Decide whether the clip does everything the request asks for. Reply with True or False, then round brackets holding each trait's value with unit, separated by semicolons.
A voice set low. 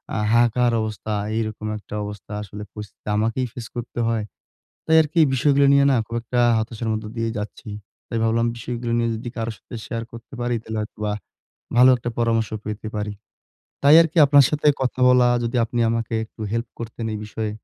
True (115 Hz)